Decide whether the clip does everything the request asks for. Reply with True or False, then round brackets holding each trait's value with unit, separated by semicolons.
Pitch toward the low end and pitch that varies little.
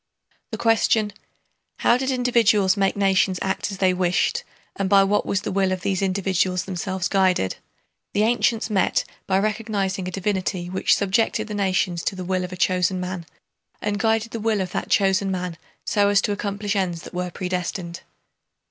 False (195 Hz; 2.1 semitones)